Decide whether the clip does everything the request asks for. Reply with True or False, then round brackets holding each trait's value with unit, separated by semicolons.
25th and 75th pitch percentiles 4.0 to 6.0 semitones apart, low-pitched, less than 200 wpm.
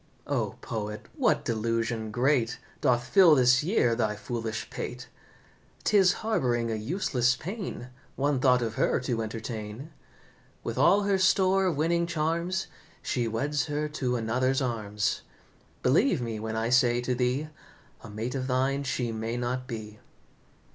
True (4.7 semitones; 125 Hz; 150 wpm)